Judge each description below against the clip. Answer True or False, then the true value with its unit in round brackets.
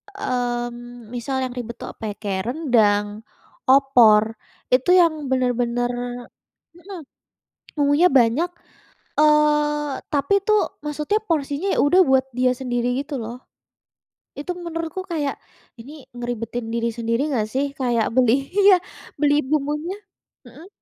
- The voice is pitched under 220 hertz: False (265 Hz)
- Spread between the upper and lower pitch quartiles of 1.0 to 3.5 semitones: False (3.9 semitones)